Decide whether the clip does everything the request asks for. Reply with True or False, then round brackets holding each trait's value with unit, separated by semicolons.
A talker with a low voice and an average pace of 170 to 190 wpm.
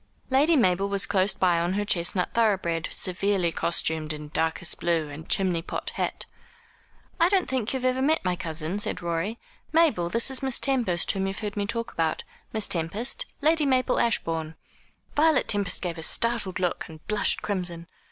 False (195 Hz; 175 wpm)